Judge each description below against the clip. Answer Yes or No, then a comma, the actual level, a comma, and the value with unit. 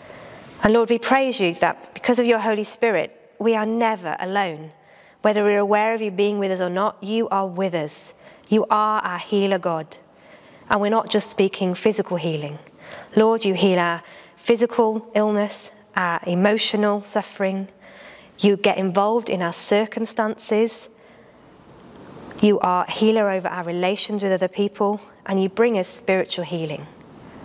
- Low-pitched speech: No, high, 205 Hz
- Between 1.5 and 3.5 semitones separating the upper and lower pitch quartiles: Yes, narrow, 2.5 semitones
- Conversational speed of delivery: Yes, average, 160 wpm